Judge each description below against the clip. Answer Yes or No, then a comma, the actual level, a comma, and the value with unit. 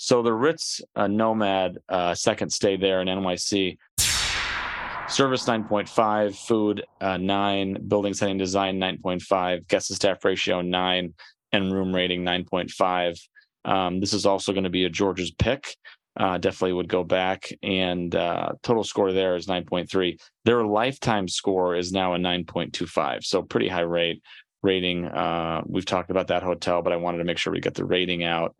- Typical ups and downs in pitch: No, narrow, 1.9 semitones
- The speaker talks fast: No, average, 170 wpm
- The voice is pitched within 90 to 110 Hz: Yes, very low, 95 Hz